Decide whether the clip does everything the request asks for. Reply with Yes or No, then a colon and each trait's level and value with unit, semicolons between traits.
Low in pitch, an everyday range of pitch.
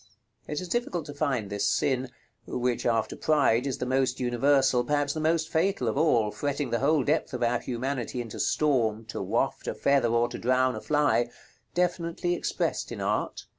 Yes: low, 130 Hz; average, 3.9 semitones